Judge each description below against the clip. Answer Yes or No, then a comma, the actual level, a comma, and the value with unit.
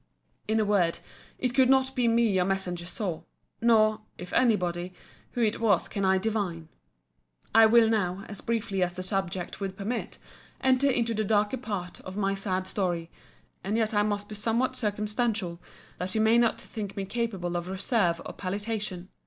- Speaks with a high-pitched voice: Yes, high, 205 Hz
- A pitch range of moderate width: Yes, average, 3.5 semitones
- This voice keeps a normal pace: Yes, average, 180 wpm